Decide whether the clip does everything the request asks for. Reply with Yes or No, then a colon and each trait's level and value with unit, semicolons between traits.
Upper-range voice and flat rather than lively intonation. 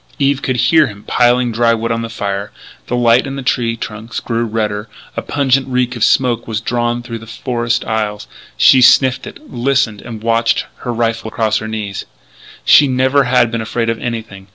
No: low, 115 Hz; narrow, 2.1 semitones